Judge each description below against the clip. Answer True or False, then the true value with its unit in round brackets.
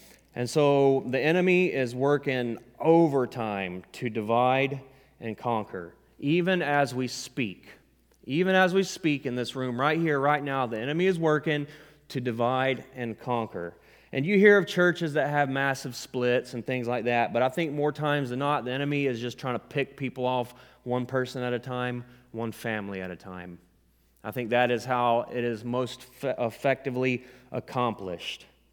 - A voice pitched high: False (125 Hz)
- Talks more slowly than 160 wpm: False (175 wpm)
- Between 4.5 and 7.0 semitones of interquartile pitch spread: False (3.3 semitones)